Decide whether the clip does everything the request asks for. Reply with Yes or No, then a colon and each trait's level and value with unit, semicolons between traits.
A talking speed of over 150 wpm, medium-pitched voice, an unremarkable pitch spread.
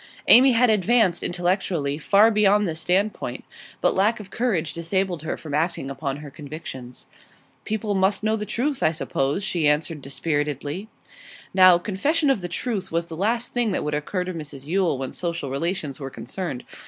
No: average, 175 wpm; medium, 175 Hz; wide, 5.7 semitones